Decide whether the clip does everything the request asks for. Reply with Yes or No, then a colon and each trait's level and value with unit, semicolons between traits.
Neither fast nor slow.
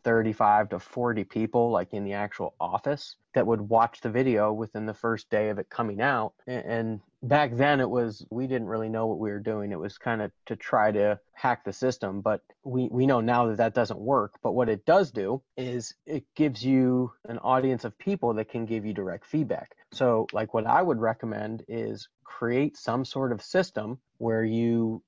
No: fast, 210 wpm